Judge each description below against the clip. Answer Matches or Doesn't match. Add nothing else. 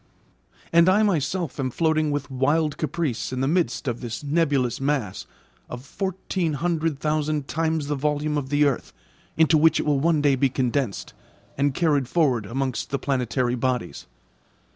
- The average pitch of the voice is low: Doesn't match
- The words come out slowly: Doesn't match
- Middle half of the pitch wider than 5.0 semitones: Doesn't match